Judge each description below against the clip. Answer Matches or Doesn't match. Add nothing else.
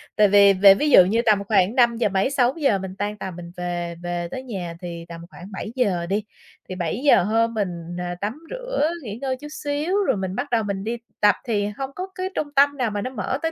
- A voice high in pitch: Matches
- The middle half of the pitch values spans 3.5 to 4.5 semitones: Doesn't match